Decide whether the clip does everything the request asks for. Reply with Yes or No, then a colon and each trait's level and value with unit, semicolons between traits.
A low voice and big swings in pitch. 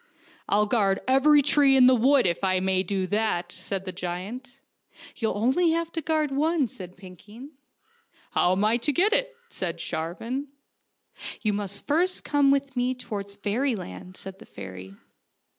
No: high, 220 Hz; wide, 6.6 semitones